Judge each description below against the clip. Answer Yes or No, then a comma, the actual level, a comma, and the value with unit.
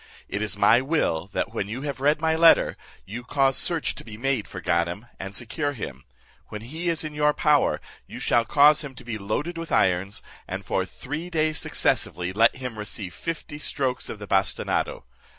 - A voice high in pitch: No, low, 125 Hz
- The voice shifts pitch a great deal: Yes, wide, 6.4 semitones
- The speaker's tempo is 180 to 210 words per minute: Yes, average, 195 wpm